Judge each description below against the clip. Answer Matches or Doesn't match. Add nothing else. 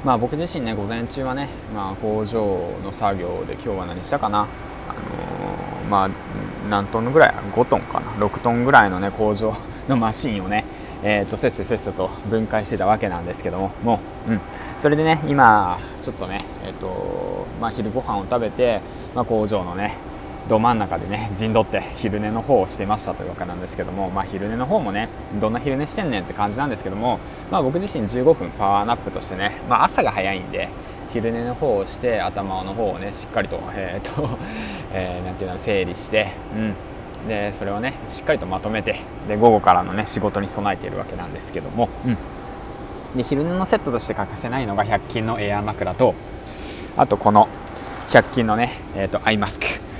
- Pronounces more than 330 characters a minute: Matches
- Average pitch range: Matches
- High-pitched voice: Doesn't match